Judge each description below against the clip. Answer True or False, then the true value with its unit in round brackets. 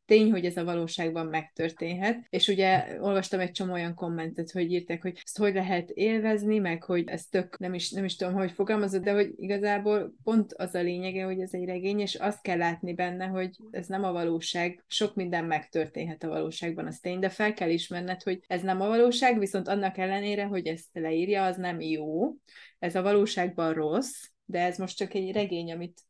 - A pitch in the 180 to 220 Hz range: True (185 Hz)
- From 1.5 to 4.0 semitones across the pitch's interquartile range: True (2.7 semitones)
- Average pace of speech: False (200 wpm)